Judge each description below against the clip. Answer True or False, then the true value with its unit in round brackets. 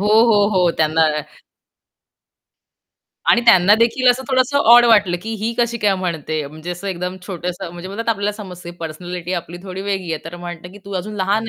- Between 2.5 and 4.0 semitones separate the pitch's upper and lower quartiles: True (3.5 semitones)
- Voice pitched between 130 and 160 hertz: False (190 Hz)